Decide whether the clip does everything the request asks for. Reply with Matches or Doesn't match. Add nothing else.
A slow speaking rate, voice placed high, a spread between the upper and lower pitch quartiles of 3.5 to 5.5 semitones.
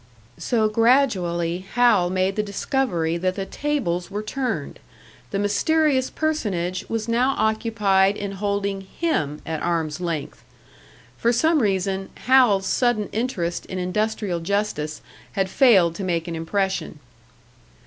Matches